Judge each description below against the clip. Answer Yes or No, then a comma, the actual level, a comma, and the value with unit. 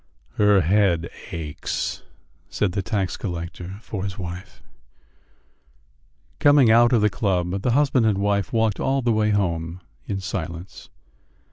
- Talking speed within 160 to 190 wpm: No, slow, 135 wpm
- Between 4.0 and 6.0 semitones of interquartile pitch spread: No, average, 3.6 semitones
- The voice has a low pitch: Yes, low, 100 Hz